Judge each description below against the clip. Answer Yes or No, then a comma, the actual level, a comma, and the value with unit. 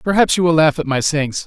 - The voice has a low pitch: No, medium, 160 Hz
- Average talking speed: No, fast, 330 wpm